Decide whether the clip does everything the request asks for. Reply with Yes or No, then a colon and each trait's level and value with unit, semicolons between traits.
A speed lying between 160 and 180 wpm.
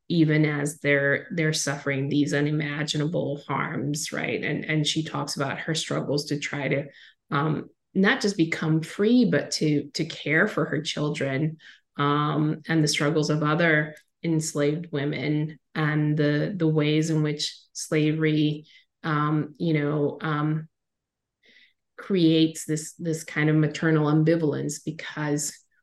No: slow, 135 wpm